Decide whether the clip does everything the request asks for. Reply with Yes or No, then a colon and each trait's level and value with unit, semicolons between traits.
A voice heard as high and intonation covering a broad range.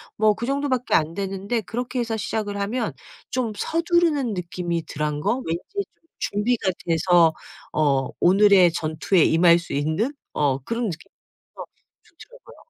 Yes: high, 200 Hz; wide, 6.2 semitones